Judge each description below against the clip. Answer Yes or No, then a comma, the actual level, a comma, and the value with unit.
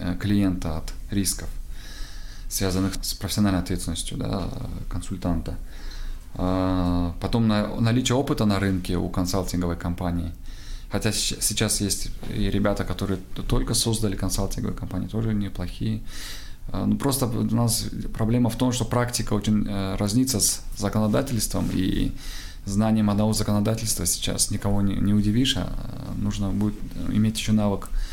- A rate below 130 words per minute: Yes, average, 120 wpm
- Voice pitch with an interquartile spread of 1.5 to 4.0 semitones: Yes, average, 3.2 semitones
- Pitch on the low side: Yes, low, 100 Hz